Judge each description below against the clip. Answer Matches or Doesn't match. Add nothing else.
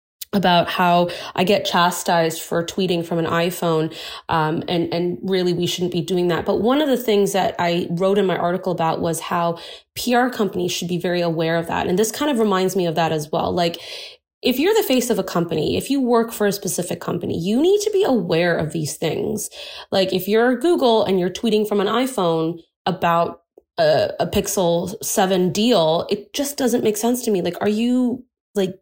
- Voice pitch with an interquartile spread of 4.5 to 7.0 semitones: Matches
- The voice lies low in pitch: Doesn't match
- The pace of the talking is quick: Matches